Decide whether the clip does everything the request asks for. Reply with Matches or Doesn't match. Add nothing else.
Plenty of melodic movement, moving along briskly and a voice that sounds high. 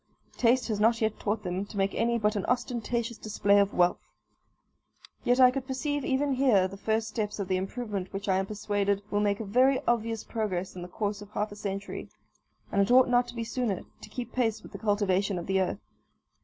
Doesn't match